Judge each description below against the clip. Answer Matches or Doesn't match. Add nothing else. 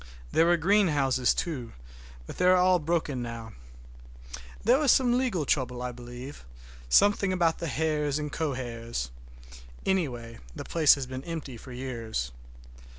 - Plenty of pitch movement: Matches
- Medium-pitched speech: Matches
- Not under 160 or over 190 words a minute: Doesn't match